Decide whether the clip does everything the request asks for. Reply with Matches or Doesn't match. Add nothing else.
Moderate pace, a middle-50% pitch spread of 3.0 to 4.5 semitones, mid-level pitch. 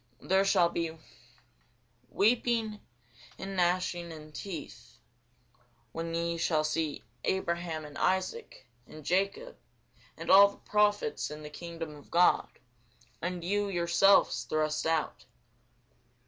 Doesn't match